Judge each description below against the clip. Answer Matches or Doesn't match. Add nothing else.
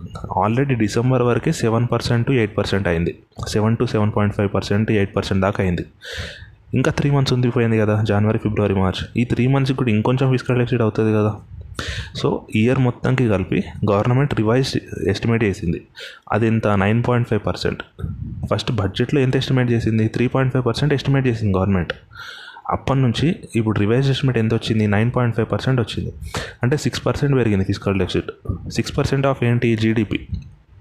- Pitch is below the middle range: Matches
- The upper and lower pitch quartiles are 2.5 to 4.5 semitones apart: Matches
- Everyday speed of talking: Doesn't match